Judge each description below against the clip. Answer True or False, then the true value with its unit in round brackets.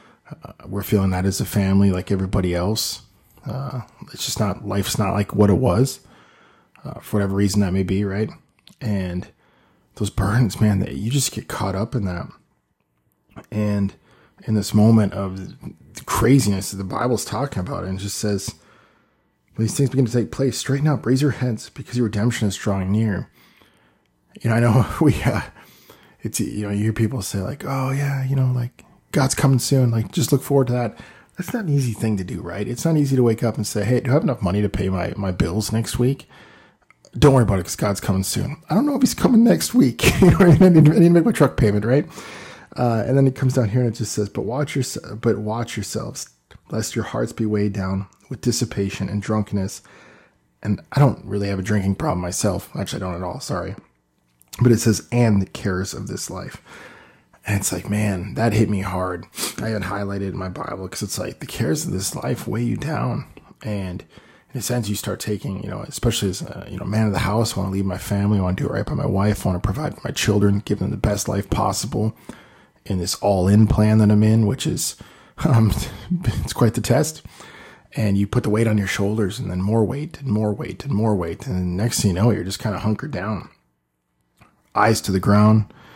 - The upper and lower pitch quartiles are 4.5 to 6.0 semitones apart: False (4.0 semitones)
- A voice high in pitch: False (105 Hz)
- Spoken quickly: True (230 wpm)